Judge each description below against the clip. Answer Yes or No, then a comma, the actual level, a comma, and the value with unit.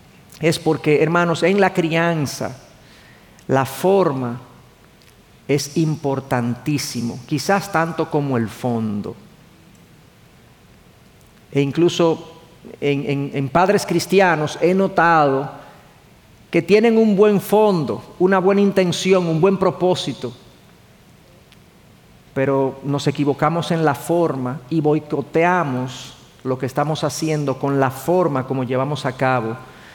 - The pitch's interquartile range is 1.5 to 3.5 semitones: No, average, 4.3 semitones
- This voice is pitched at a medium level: Yes, medium, 150 Hz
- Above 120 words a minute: No, slow, 110 wpm